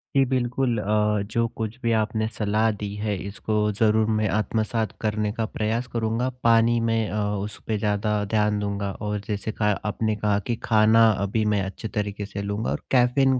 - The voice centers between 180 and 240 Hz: No, low, 110 Hz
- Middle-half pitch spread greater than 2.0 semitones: No, narrow, 1.5 semitones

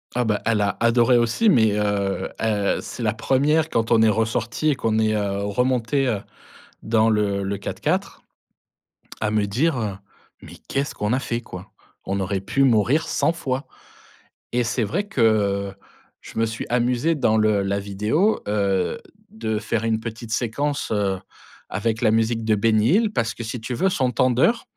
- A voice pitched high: No, low, 115 Hz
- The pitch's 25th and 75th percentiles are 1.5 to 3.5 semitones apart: Yes, average, 3.1 semitones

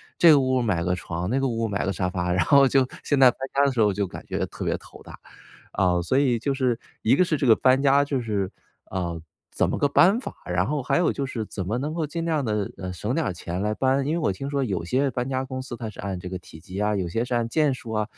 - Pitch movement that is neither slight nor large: No, wide, 6.0 semitones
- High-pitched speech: No, low, 120 Hz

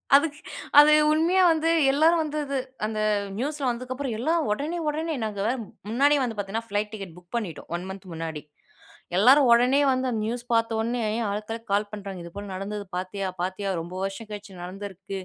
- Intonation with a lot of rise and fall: Yes, wide, 5.8 semitones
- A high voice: Yes, high, 220 Hz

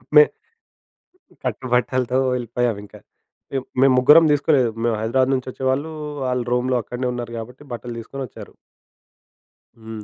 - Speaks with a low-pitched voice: Yes, low, 125 Hz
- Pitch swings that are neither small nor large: No, narrow, 2.0 semitones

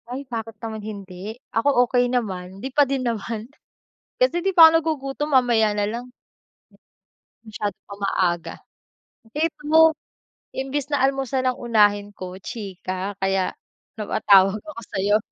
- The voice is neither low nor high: No, high, 225 Hz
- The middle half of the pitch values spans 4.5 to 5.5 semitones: Yes, average, 4.9 semitones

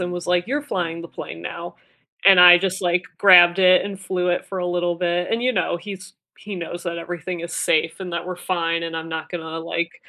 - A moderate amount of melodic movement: No, narrow, 1.5 semitones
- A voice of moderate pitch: Yes, medium, 175 Hz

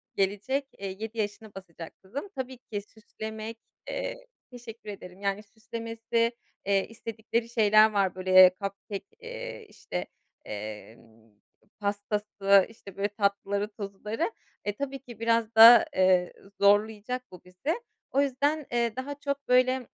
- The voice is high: Yes, high, 215 Hz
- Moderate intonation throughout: Yes, average, 3.5 semitones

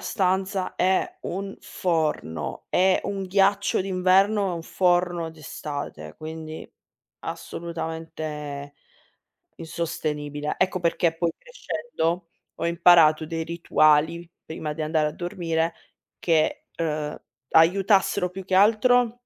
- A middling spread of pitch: Yes, average, 3.1 semitones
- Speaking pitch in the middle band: Yes, medium, 170 Hz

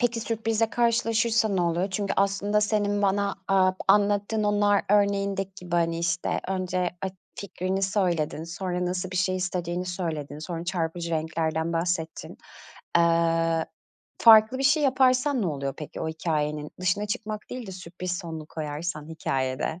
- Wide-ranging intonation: No, average, 3.7 semitones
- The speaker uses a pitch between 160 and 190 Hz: Yes, medium, 185 Hz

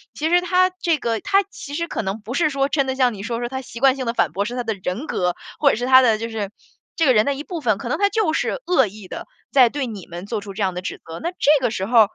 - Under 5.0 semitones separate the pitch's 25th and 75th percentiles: No, wide, 5.4 semitones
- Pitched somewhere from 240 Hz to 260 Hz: Yes, high, 245 Hz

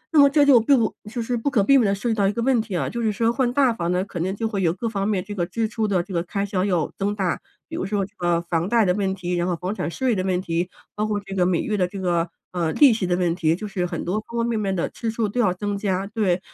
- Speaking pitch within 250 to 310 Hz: No, high, 200 Hz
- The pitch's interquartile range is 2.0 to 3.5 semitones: No, average, 3.9 semitones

